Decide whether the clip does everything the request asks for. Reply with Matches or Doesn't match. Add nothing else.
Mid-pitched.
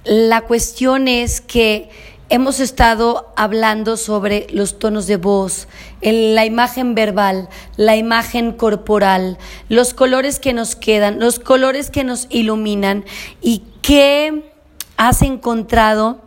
Doesn't match